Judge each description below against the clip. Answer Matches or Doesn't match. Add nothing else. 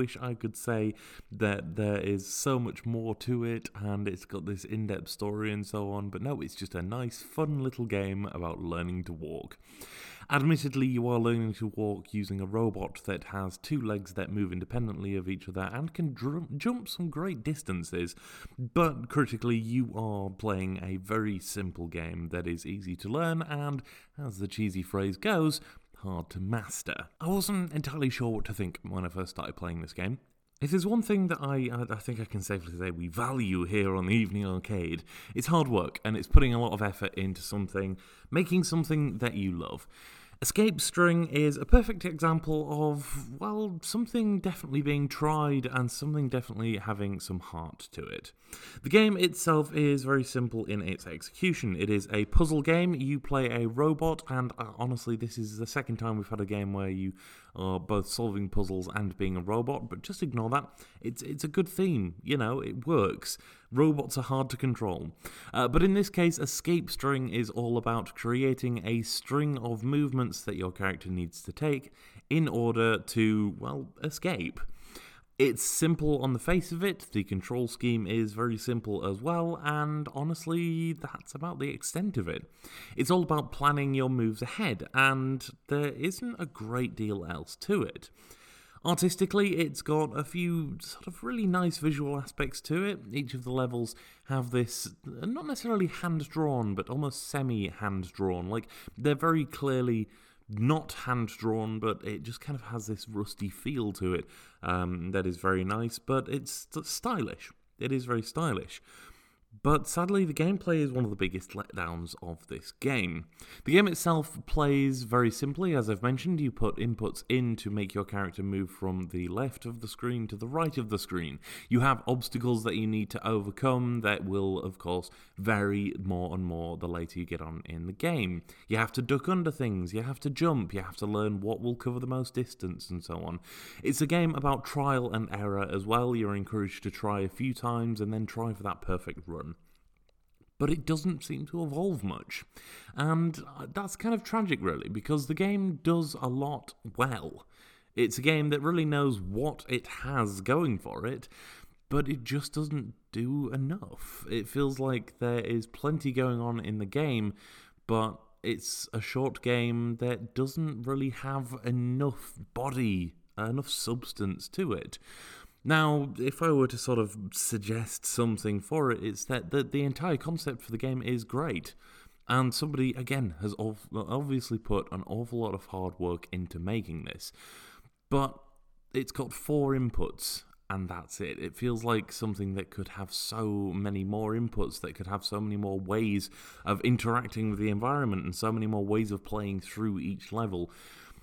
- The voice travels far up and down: Matches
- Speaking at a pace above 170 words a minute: Matches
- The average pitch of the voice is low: Matches